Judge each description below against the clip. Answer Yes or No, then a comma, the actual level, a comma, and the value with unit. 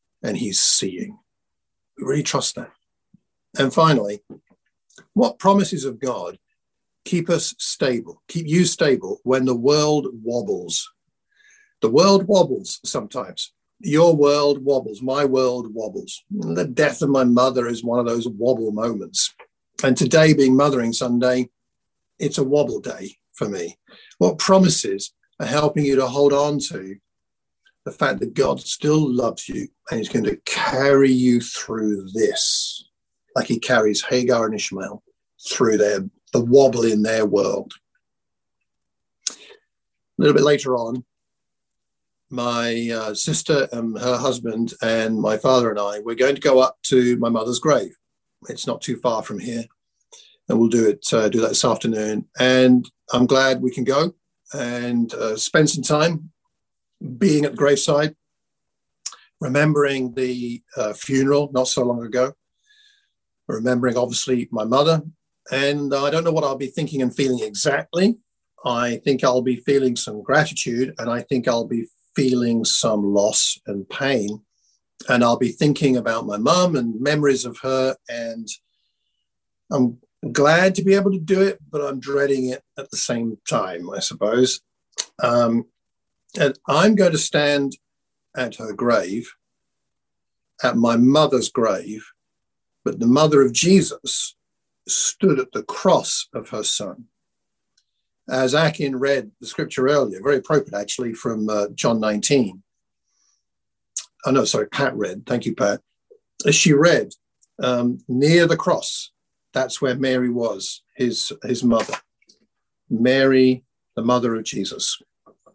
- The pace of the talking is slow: No, average, 145 wpm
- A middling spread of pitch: Yes, average, 3.8 semitones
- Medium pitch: No, low, 130 Hz